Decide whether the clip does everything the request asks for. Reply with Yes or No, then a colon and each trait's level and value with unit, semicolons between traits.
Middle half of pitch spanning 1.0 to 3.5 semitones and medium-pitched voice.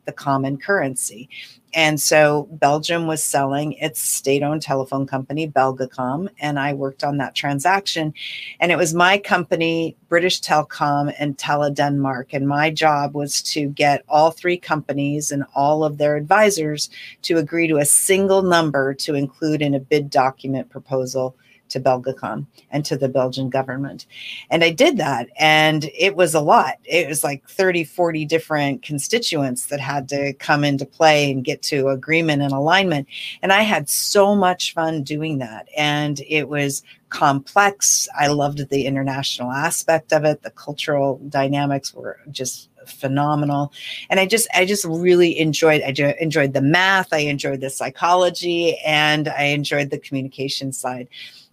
Yes: average, 2.8 semitones; medium, 145 Hz